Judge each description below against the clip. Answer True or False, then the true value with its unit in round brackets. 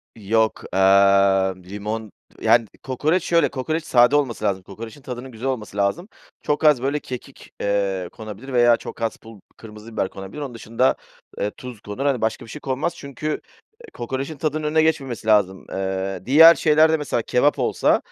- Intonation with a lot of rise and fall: True (5.7 semitones)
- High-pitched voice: False (120 Hz)